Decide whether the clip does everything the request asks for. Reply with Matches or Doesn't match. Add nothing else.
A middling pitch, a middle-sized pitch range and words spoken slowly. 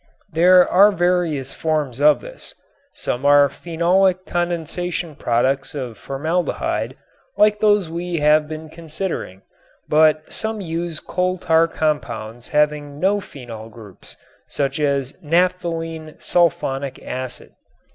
Matches